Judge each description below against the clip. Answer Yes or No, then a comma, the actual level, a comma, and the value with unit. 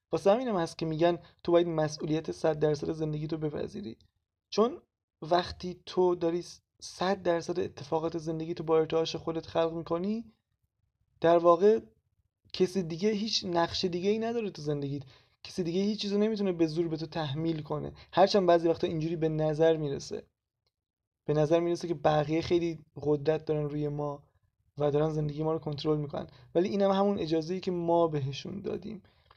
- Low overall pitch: No, medium, 165 Hz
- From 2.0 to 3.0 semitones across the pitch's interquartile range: Yes, average, 2.7 semitones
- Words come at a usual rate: No, fast, 170 wpm